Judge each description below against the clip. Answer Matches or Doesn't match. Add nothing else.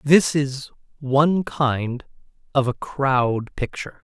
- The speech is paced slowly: Matches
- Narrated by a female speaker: Doesn't match